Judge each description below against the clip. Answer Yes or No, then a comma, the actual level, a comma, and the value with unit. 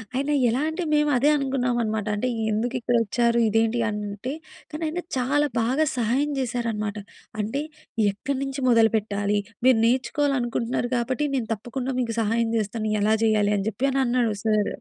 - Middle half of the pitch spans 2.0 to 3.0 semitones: No, average, 3.4 semitones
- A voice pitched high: Yes, high, 240 Hz